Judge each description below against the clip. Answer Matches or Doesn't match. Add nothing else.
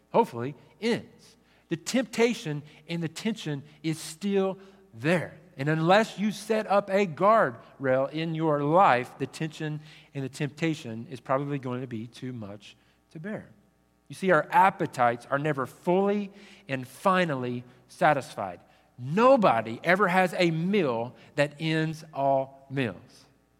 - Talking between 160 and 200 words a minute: Doesn't match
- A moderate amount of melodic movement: Doesn't match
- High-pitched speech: Doesn't match